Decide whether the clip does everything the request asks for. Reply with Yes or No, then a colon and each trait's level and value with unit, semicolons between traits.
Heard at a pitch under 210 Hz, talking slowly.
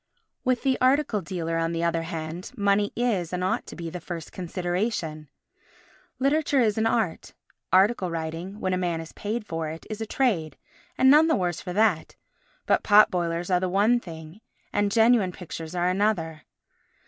No: medium, 185 Hz; average, 175 wpm